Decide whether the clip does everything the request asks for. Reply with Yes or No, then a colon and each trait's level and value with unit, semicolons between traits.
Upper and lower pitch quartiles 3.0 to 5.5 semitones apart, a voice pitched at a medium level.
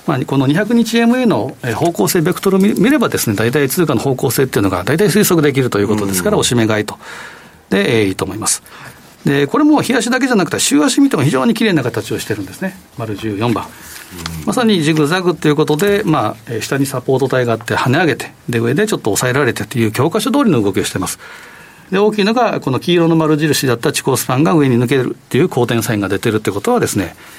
No: wide, 8.7 semitones; medium, 145 Hz